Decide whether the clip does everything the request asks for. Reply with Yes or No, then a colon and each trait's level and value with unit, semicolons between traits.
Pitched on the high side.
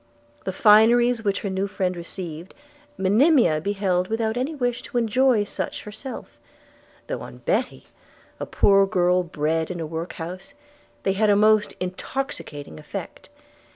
Yes: high, 200 Hz